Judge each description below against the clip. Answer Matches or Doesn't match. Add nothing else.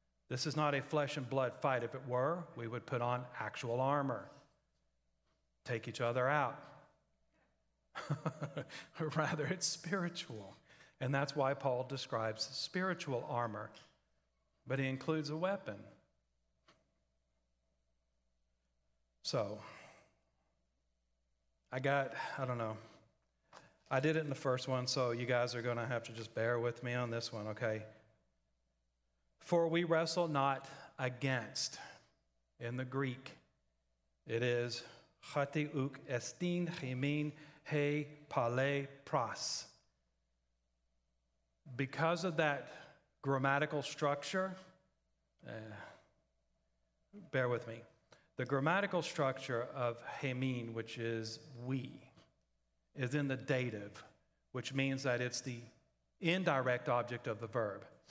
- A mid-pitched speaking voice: Doesn't match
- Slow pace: Matches